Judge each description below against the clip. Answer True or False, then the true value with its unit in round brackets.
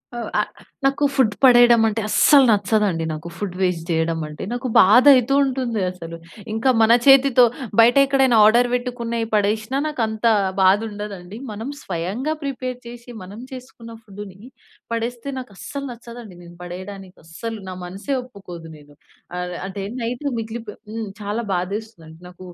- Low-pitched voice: False (220 Hz)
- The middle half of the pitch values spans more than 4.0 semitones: True (4.7 semitones)